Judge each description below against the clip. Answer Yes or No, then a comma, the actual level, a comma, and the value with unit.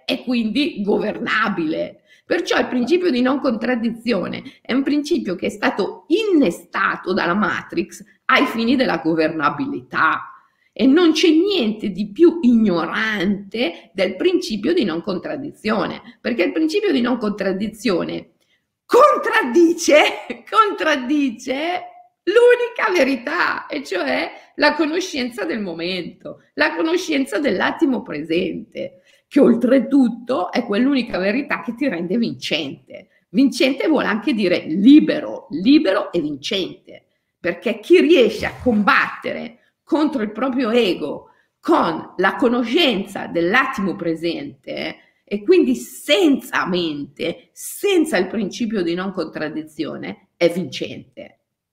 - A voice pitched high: Yes, very high, 255 Hz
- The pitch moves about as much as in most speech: No, wide, 7.1 semitones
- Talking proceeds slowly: Yes, slow, 110 wpm